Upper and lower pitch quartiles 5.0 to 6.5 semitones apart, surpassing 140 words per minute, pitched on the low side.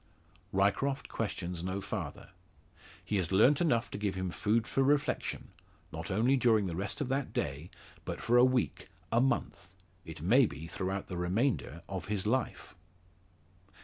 Yes: wide, 5.4 semitones; average, 160 wpm; low, 105 Hz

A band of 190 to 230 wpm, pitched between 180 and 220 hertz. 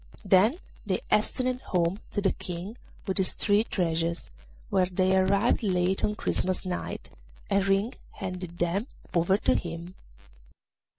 No: slow, 135 wpm; high, 190 Hz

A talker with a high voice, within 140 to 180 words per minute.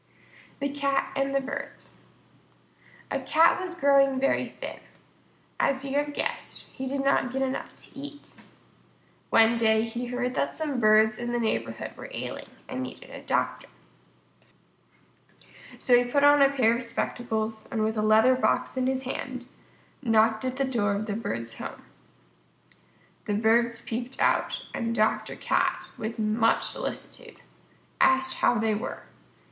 Yes: high, 245 Hz; average, 155 wpm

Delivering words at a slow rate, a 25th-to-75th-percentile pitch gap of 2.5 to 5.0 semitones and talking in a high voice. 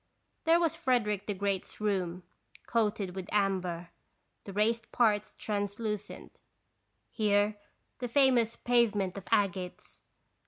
Yes: slow, 110 wpm; average, 2.8 semitones; high, 210 Hz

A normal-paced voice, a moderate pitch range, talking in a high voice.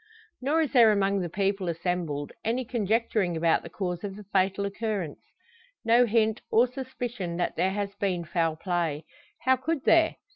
Yes: average, 170 wpm; average, 4.8 semitones; high, 200 Hz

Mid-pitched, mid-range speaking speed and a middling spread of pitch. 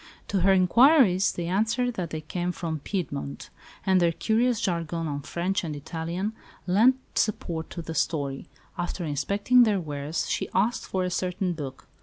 Yes: medium, 180 Hz; average, 165 wpm; average, 3.7 semitones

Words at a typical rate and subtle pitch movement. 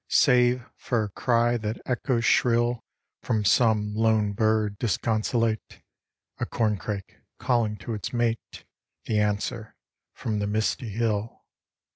No: slow, 120 wpm; narrow, 2.0 semitones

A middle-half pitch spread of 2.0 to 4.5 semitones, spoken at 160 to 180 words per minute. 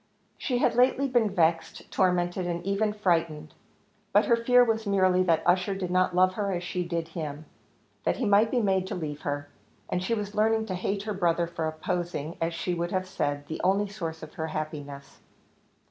No: average, 3.7 semitones; average, 200 wpm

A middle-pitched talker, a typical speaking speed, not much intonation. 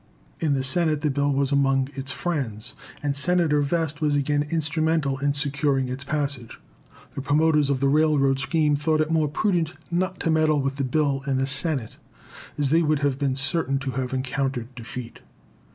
Yes: medium, 145 Hz; average, 185 wpm; narrow, 2.3 semitones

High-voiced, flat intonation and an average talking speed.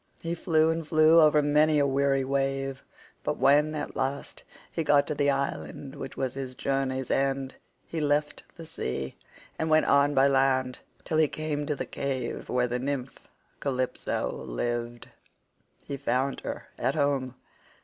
No: medium, 140 Hz; narrow, 2.2 semitones; average, 160 wpm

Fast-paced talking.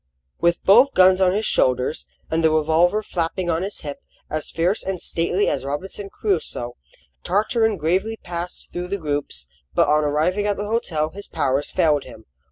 No: average, 175 wpm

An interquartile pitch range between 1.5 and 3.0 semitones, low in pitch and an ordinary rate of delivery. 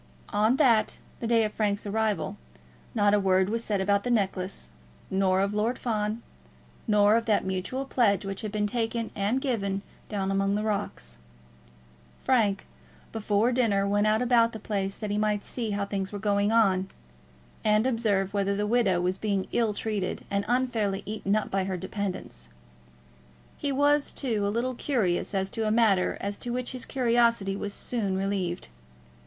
No: narrow, 2.6 semitones; high, 210 Hz; average, 175 wpm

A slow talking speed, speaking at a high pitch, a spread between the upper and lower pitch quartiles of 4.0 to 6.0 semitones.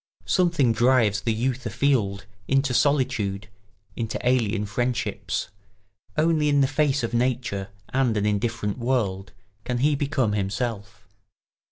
No: slow, 125 wpm; low, 120 Hz; average, 4.4 semitones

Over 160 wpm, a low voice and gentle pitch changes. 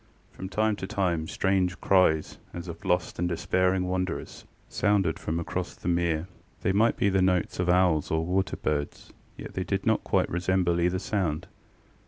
Yes: average, 175 wpm; very low, 90 Hz; narrow, 1.8 semitones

